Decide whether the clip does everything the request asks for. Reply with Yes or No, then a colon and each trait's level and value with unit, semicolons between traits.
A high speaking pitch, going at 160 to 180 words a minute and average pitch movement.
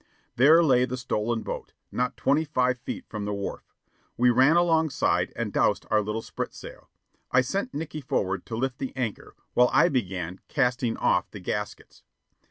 No: low, 125 Hz; average, 170 wpm; average, 4.2 semitones